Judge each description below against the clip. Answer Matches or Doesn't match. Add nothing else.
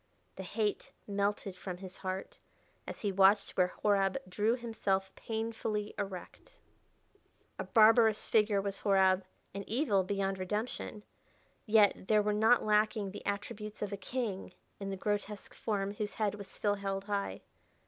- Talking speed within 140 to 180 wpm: Matches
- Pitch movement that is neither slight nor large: Doesn't match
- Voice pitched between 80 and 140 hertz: Doesn't match